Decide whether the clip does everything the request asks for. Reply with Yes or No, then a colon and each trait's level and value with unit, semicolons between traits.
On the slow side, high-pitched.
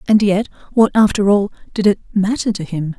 No: average, 200 wpm; high, 200 Hz